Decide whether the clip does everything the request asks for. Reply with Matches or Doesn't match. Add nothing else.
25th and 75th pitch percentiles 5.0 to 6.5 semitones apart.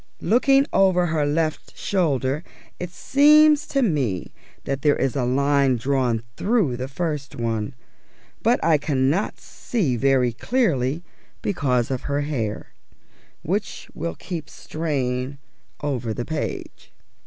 Matches